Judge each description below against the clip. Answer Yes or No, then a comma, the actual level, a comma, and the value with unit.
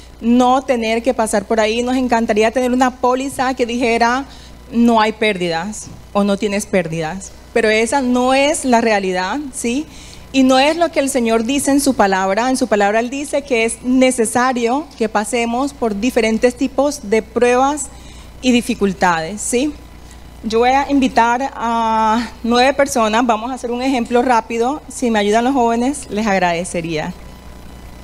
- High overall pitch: Yes, high, 235 Hz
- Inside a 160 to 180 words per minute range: Yes, average, 165 wpm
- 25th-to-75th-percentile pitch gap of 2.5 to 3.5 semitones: Yes, average, 3.1 semitones